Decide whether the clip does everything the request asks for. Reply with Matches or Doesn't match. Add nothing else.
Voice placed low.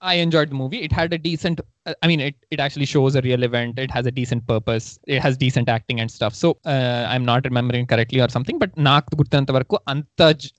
Matches